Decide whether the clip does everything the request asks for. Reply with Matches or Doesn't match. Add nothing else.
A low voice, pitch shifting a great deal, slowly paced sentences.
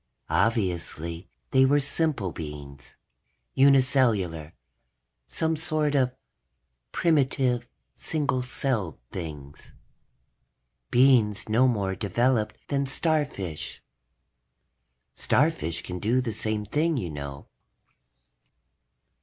Matches